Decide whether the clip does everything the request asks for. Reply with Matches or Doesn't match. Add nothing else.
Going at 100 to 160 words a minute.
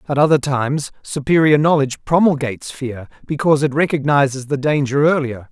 Matches